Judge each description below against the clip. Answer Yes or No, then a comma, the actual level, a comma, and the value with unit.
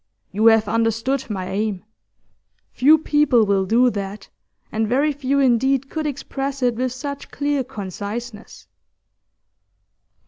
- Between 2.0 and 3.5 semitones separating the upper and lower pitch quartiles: No, average, 4.4 semitones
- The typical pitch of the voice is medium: No, high, 240 Hz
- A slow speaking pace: Yes, slow, 125 wpm